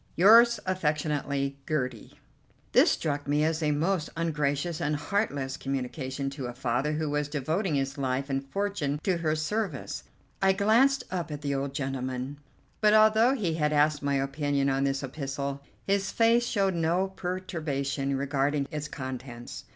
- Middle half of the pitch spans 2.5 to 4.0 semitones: No, average, 4.7 semitones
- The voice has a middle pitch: Yes, medium, 150 Hz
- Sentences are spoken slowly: No, average, 155 wpm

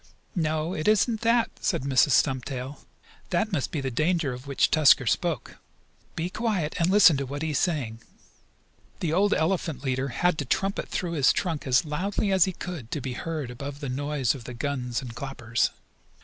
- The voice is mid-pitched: Yes, medium, 150 Hz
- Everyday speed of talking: Yes, average, 190 wpm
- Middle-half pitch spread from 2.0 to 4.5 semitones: No, average, 5.0 semitones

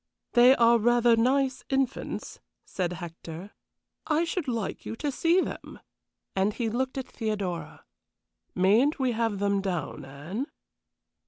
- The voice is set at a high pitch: Yes, high, 230 Hz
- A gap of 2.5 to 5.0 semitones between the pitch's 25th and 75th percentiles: No, wide, 5.4 semitones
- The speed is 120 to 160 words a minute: Yes, slow, 135 wpm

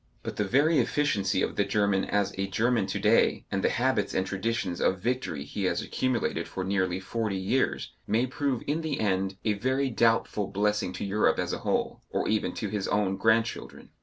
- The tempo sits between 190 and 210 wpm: Yes, average, 195 wpm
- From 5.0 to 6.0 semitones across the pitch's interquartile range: No, average, 3.5 semitones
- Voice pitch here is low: Yes, low, 105 Hz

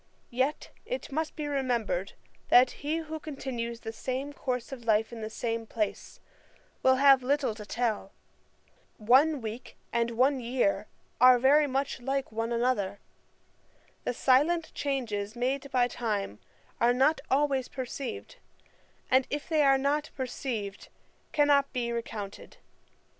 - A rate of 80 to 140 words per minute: Yes, slow, 135 wpm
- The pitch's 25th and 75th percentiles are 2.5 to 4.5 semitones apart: Yes, average, 3.3 semitones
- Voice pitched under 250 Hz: No, very high, 255 Hz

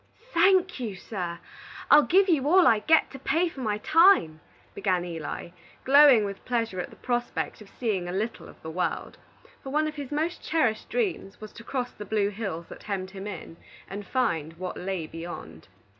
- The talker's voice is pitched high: Yes, high, 220 Hz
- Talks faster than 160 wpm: Yes, average, 190 wpm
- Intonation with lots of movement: Yes, wide, 7.9 semitones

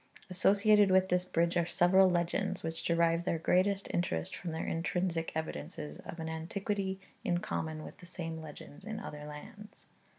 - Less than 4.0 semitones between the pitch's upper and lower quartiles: Yes, average, 2.8 semitones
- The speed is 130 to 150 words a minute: No, average, 165 wpm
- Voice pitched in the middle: Yes, medium, 175 Hz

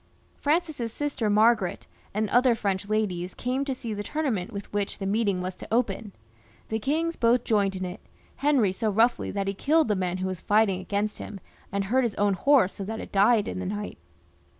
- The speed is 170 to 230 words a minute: Yes, fast, 205 wpm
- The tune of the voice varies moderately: Yes, average, 3.7 semitones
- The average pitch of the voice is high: Yes, high, 210 Hz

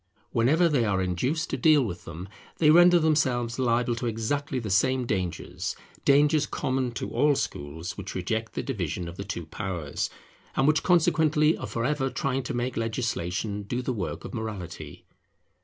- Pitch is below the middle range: Yes, low, 120 Hz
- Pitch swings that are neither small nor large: No, wide, 6.5 semitones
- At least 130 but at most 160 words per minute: No, average, 175 wpm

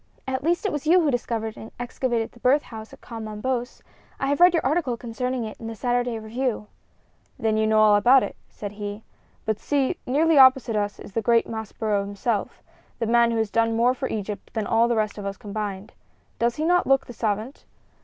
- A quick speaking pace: Yes, fast, 215 wpm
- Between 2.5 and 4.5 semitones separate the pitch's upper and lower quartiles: Yes, average, 3.2 semitones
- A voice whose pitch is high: Yes, high, 230 Hz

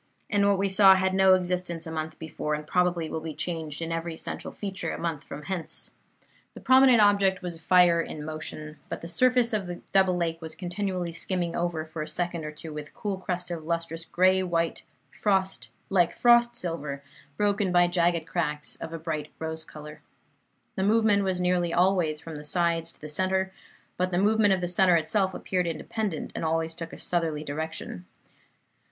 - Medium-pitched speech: Yes, medium, 175 Hz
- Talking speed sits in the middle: Yes, average, 190 wpm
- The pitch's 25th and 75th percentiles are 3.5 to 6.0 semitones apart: No, average, 2.8 semitones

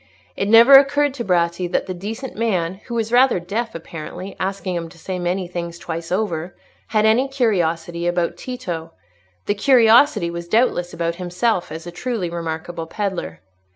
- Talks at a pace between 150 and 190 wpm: Yes, average, 165 wpm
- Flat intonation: No, average, 4.9 semitones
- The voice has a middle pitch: Yes, medium, 180 Hz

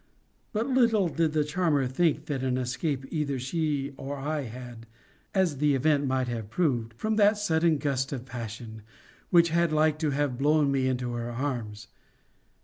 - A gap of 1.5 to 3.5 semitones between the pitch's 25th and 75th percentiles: No, average, 3.9 semitones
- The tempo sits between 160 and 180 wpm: Yes, average, 170 wpm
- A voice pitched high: No, medium, 140 Hz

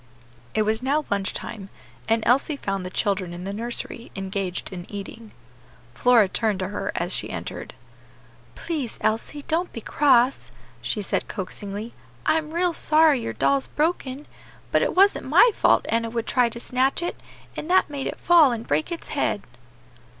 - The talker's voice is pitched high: Yes, high, 230 Hz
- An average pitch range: No, wide, 6.7 semitones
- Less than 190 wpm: Yes, average, 170 wpm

